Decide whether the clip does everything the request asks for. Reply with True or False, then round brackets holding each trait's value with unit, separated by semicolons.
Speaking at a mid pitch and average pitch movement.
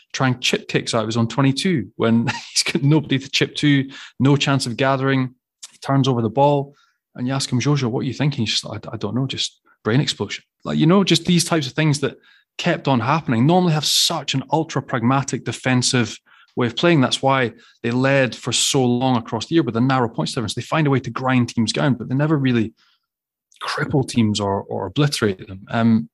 False (130 Hz; 3.3 semitones)